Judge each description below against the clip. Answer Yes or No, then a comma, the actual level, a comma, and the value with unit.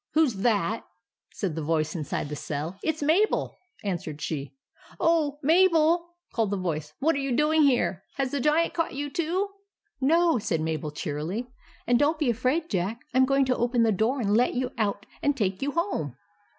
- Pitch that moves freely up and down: Yes, wide, 8.5 semitones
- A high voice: Yes, very high, 250 Hz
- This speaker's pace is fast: Yes, fast, 225 wpm